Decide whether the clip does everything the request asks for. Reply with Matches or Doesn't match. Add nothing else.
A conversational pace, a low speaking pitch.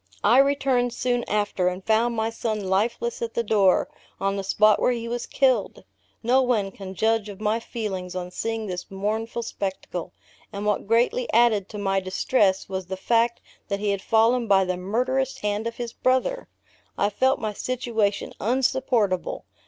Doesn't match